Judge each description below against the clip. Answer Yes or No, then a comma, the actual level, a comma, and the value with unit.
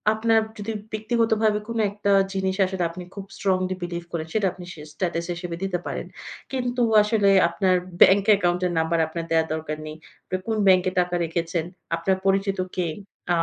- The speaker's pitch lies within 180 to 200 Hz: Yes, medium, 185 Hz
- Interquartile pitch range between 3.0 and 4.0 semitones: Yes, average, 3.4 semitones